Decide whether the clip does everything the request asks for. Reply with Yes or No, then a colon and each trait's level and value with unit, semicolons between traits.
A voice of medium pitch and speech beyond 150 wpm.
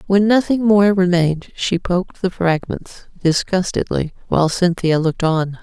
No: medium, 180 Hz; average, 140 wpm